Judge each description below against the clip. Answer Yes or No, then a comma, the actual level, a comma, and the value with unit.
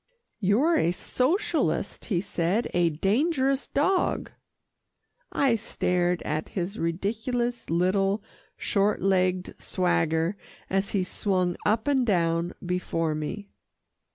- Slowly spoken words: Yes, slow, 105 wpm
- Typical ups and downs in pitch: Yes, average, 4.9 semitones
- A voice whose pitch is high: Yes, high, 195 Hz